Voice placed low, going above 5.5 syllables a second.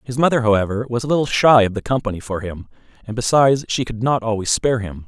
Yes: low, 115 Hz; 6.6 syllables/s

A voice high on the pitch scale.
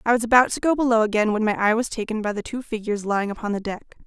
Yes: high, 220 Hz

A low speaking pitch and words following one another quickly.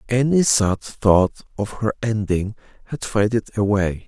No: low, 110 Hz; slow, 135 wpm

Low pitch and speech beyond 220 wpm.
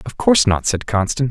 Yes: low, 120 Hz; fast, 230 wpm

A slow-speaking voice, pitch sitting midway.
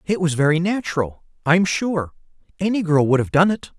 No: average, 190 wpm; medium, 170 Hz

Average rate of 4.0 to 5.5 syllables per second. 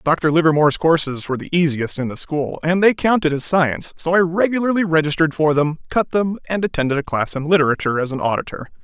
No: 6.3 syllables/s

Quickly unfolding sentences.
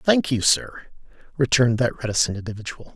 No: average, 140 wpm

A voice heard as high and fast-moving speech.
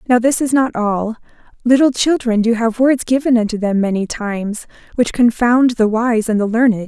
No: high, 235 Hz; average, 190 wpm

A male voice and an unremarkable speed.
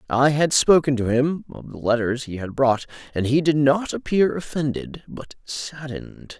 Yes: male; average, 180 wpm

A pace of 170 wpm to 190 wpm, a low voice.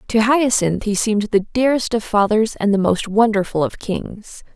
No: average, 185 wpm; high, 215 Hz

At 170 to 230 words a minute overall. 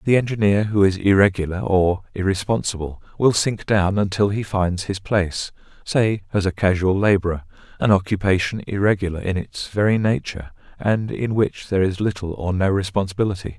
No: average, 160 wpm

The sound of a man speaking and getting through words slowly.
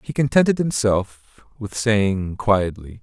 Yes: male; slow, 120 wpm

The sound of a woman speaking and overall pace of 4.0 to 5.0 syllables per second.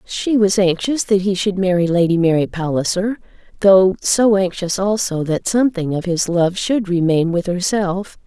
Yes: female; 4.6 syllables/s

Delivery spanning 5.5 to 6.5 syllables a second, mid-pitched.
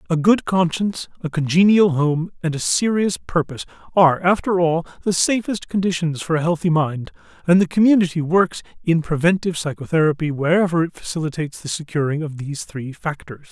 Yes: 5.7 syllables/s; medium, 165 Hz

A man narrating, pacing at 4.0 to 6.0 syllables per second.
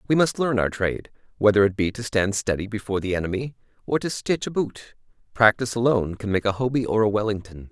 No: male; 6.4 syllables/s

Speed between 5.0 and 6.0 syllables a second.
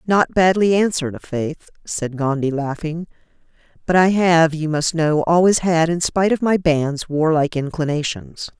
No: 4.8 syllables/s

